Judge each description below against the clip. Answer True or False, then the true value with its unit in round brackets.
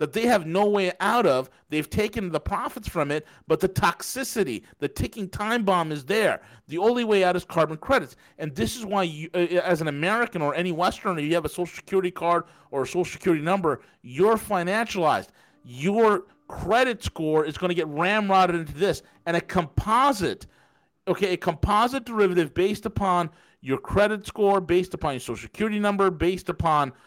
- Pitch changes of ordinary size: True (4.2 semitones)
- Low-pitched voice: False (180 Hz)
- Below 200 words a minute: True (185 wpm)